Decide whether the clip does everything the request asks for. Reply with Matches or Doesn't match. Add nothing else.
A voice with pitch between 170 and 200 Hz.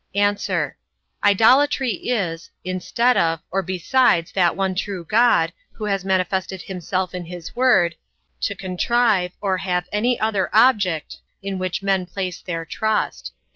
Matches